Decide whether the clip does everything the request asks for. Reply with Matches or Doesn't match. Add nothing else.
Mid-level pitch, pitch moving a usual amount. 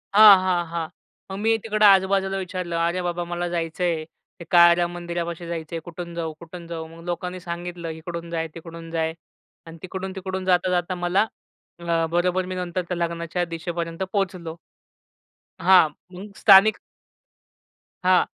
Doesn't match